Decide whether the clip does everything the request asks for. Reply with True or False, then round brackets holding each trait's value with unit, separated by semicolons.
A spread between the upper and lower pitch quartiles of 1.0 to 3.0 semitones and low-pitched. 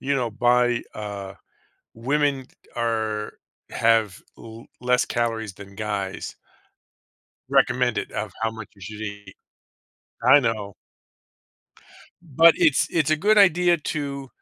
False (4.7 semitones; 115 Hz)